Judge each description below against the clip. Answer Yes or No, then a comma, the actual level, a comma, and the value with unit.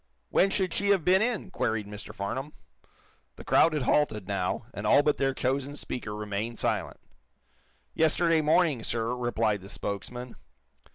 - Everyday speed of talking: Yes, average, 155 wpm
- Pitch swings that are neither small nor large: No, wide, 6.8 semitones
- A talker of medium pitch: No, low, 125 Hz